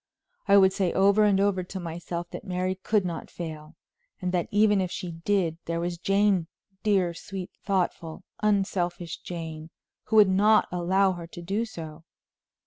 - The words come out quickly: No, average, 165 wpm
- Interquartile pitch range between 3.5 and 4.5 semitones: No, narrow, 2.6 semitones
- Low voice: No, medium, 185 Hz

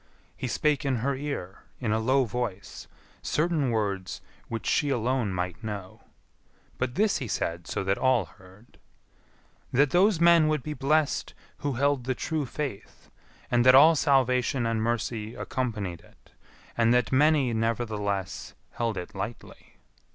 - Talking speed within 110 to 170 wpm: Yes, average, 150 wpm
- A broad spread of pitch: No, average, 4.8 semitones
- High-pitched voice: No, low, 120 Hz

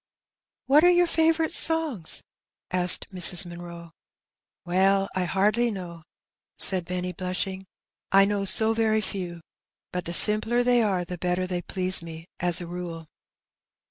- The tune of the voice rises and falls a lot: No, average, 3.6 semitones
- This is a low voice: No, medium, 185 Hz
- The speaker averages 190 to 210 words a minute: No, average, 160 wpm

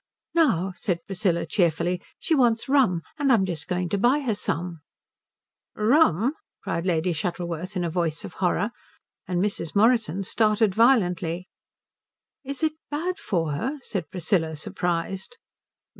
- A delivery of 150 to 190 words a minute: No, average, 140 wpm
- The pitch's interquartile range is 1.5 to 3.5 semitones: No, average, 5.2 semitones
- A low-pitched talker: No, medium, 185 Hz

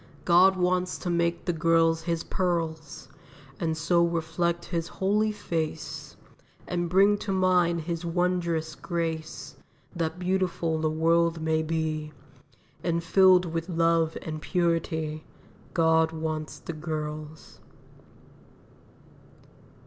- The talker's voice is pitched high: No, medium, 165 Hz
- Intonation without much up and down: Yes, narrow, 1.7 semitones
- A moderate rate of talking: No, slow, 110 wpm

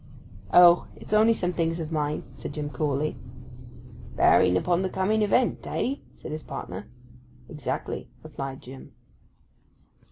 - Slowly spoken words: Yes, slow, 120 wpm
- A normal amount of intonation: Yes, average, 5.0 semitones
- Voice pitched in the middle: Yes, medium, 160 Hz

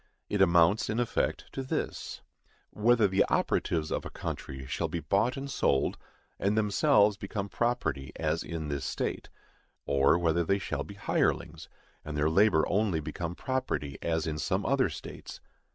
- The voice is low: Yes, very low, 95 Hz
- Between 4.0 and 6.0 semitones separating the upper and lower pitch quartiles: Yes, average, 5.1 semitones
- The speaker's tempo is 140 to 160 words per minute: Yes, average, 155 wpm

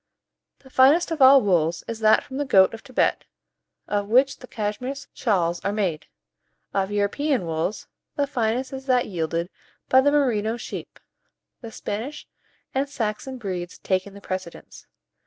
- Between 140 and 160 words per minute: Yes, average, 155 wpm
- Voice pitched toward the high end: Yes, high, 220 Hz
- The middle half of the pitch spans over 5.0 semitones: Yes, wide, 5.4 semitones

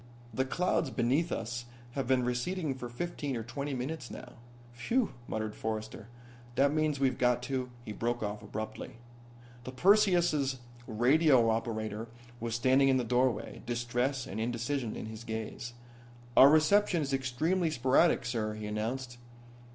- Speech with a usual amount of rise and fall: Yes, average, 3.5 semitones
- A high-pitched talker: No, low, 125 Hz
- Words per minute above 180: No, average, 150 wpm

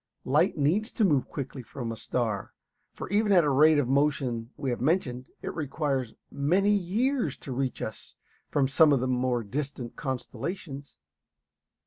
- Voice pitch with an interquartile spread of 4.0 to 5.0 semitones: Yes, average, 4.3 semitones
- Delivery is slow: No, average, 165 wpm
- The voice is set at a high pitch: No, medium, 140 Hz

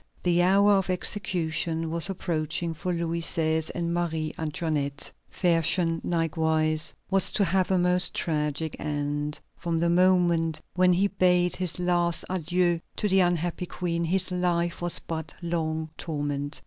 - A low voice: No, medium, 170 Hz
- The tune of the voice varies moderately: No, narrow, 2.0 semitones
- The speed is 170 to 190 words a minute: No, average, 150 wpm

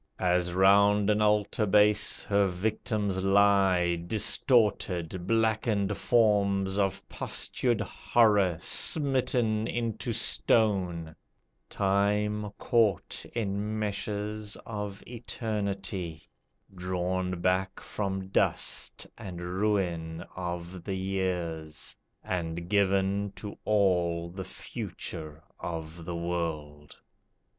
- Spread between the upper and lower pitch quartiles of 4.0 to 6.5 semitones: No, average, 3.0 semitones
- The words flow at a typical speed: No, slow, 90 wpm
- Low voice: Yes, very low, 95 Hz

